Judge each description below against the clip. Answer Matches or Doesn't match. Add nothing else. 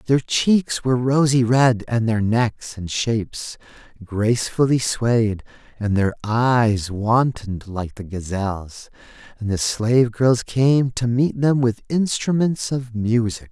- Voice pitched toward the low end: Matches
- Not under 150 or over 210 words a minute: Doesn't match